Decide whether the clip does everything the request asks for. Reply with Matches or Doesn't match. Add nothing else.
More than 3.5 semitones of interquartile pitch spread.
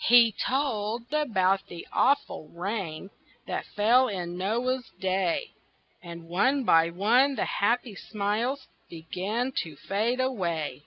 Matches